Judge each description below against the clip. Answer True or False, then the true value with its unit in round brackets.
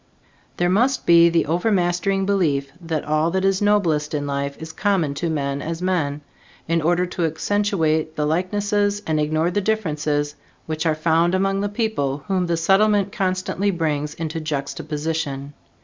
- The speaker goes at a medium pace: True (160 wpm)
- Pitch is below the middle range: False (165 Hz)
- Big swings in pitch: False (4.2 semitones)